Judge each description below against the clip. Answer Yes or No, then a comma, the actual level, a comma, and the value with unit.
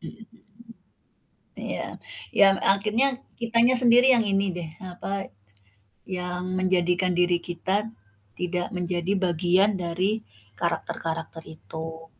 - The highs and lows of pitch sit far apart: No, average, 2.7 semitones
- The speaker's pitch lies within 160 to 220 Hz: Yes, medium, 185 Hz